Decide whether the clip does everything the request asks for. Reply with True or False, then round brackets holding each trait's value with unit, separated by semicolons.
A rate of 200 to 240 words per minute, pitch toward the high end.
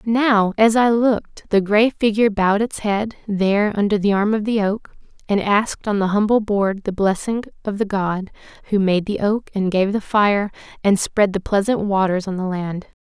True (205 wpm; 205 Hz)